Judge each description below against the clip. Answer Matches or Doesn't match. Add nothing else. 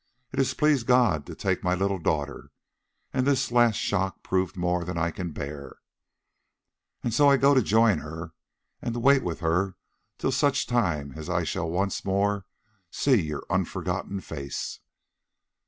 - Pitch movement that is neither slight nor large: Doesn't match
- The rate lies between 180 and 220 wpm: Doesn't match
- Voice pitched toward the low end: Matches